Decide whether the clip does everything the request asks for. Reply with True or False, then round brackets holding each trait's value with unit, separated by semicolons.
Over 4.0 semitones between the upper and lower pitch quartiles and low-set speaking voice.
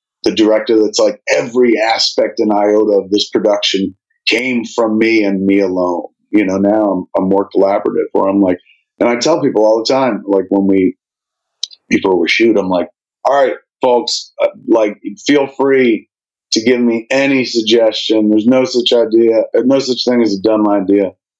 False (3.2 semitones; 110 Hz)